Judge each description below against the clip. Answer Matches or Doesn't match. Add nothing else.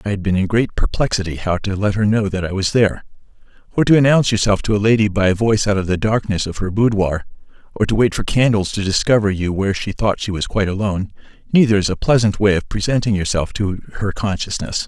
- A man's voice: Matches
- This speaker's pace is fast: Matches